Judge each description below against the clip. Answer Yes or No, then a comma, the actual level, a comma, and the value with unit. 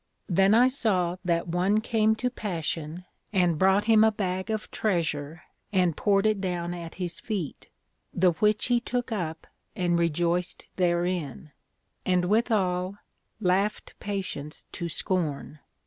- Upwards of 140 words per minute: No, slow, 135 wpm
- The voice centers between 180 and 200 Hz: Yes, medium, 185 Hz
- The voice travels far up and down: No, average, 3.6 semitones